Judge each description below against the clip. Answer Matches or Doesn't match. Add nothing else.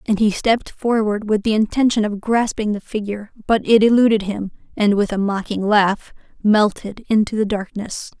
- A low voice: Doesn't match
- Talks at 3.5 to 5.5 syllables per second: Matches